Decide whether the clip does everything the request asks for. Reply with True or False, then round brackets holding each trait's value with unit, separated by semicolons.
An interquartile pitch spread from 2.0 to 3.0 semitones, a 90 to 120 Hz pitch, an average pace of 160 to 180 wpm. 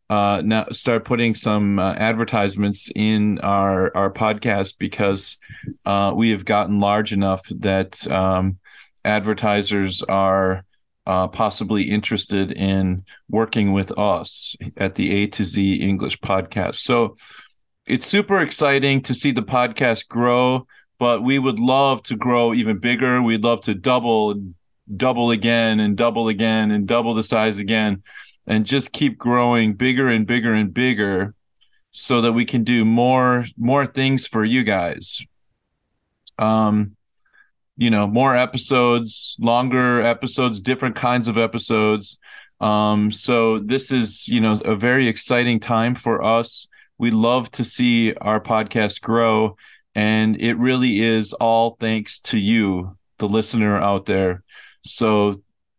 False (2.7 semitones; 110 Hz; 140 wpm)